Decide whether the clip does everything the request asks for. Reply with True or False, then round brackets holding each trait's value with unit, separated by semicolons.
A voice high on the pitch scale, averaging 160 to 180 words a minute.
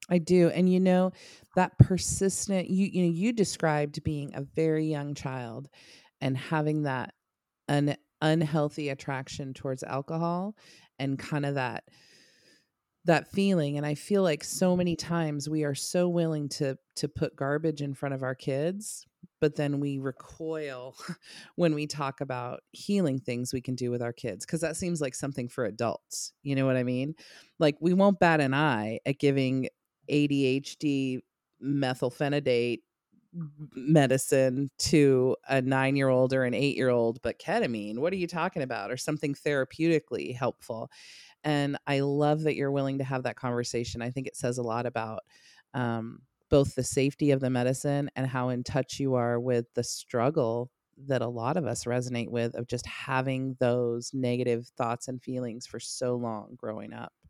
False (140 Hz; 175 wpm)